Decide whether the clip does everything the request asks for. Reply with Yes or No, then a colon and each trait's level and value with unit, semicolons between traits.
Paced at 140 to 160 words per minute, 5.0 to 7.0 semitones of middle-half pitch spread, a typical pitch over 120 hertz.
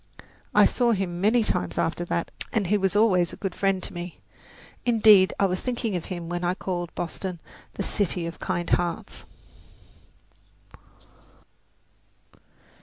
No: average, 145 wpm; average, 2.9 semitones; medium, 185 Hz